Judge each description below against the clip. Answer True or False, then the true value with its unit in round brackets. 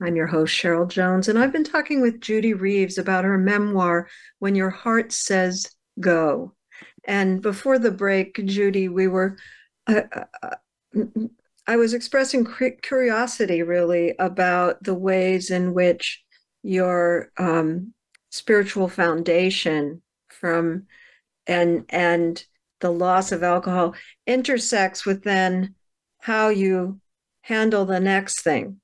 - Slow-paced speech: True (120 wpm)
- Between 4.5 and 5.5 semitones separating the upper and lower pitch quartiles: False (3.5 semitones)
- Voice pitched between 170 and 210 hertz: True (190 Hz)